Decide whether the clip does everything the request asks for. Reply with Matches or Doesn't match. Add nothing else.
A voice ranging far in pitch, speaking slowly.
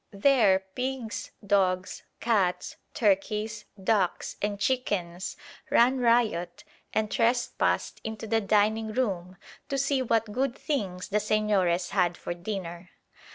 Doesn't match